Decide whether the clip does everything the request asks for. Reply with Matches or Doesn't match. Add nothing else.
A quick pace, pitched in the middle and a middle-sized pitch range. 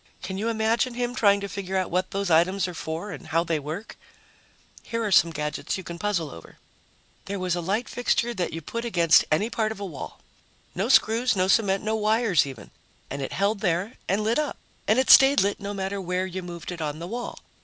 Doesn't match